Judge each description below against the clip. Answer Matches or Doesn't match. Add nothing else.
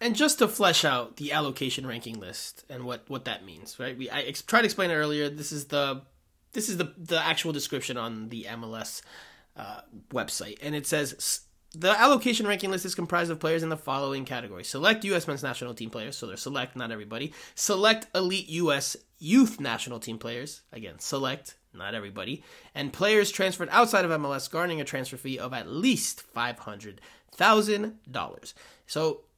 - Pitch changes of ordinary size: Doesn't match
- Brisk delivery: Doesn't match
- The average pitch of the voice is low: Doesn't match